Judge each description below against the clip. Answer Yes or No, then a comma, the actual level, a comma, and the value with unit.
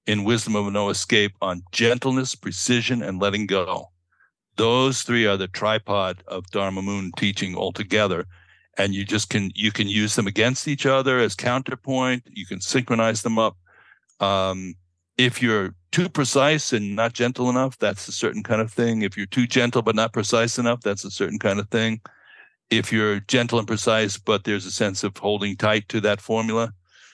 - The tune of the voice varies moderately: Yes, average, 3.2 semitones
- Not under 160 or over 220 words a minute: Yes, average, 185 wpm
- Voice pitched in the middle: No, low, 110 Hz